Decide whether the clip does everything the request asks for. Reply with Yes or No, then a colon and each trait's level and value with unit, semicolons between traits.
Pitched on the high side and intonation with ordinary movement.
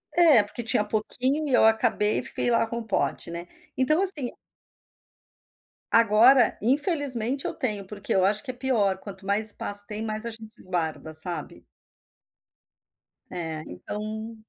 Yes: high, 220 Hz; average, 3.9 semitones